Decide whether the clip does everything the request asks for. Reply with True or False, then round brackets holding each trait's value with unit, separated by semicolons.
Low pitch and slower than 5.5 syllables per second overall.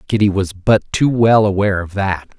True (100 Hz; 5.1 syllables/s)